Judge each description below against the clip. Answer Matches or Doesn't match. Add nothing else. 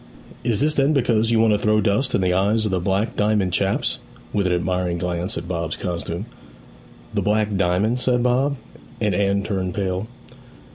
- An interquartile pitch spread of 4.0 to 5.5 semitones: Doesn't match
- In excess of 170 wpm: Matches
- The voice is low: Matches